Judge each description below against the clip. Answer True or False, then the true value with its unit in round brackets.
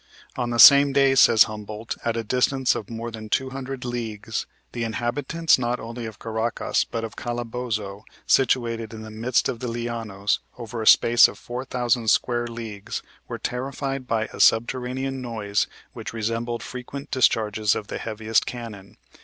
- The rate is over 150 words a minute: True (160 wpm)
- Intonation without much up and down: True (2.1 semitones)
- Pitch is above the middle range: False (115 Hz)